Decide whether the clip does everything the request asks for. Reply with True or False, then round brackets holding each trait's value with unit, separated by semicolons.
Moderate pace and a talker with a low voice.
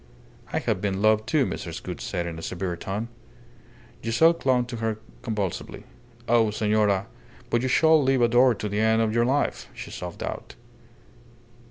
True (170 wpm; 110 Hz)